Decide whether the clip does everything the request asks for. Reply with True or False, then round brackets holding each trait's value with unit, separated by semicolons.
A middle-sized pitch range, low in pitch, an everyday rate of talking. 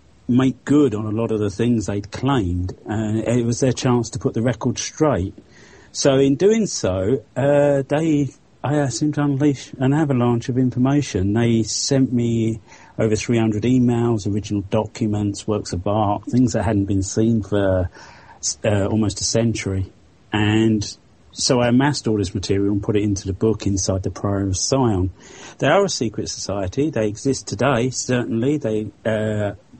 True (4.0 semitones; 110 Hz; 175 wpm)